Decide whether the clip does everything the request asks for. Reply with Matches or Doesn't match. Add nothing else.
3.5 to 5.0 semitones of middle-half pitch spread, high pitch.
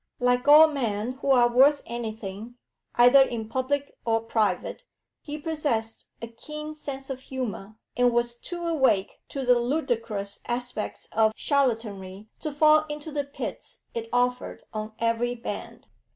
Matches